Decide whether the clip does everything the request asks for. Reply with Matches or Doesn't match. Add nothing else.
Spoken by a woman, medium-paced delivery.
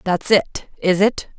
Matches